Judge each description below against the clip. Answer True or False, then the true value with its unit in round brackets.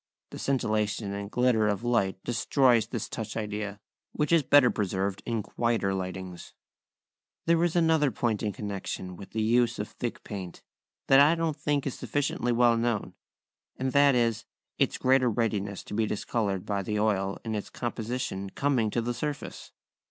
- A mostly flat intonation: False (3.8 semitones)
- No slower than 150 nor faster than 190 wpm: True (165 wpm)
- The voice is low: True (115 Hz)